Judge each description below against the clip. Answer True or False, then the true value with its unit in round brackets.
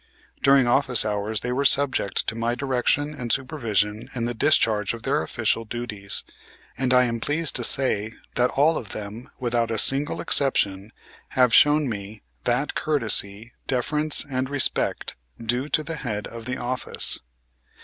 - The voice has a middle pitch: False (120 Hz)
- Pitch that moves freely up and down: False (3.8 semitones)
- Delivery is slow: False (160 wpm)